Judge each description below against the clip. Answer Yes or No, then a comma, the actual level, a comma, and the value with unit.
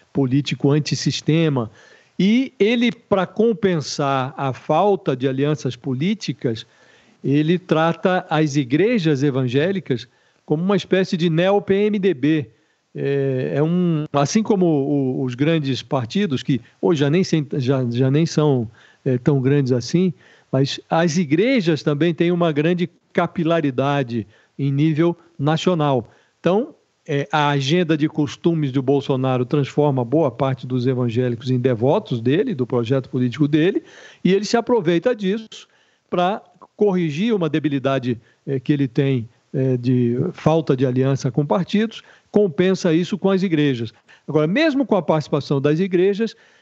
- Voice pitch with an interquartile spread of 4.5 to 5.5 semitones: Yes, average, 5.1 semitones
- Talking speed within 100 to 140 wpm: Yes, average, 135 wpm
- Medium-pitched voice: Yes, medium, 150 Hz